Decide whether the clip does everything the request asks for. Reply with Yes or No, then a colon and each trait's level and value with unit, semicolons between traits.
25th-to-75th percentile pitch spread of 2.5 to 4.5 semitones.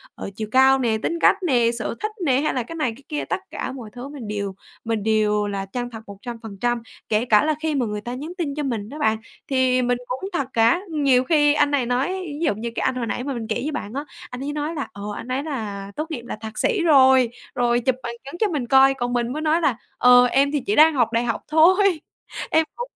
Yes: average, 4.2 semitones